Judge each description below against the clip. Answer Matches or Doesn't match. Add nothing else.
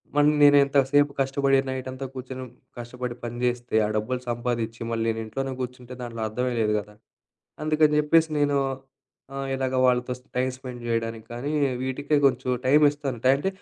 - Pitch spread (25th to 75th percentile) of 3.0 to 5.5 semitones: Doesn't match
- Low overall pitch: Matches